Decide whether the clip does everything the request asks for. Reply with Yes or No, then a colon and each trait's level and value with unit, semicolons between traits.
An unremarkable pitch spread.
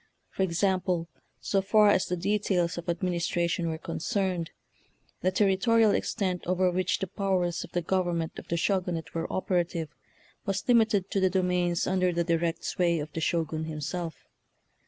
No: narrow, 2.1 semitones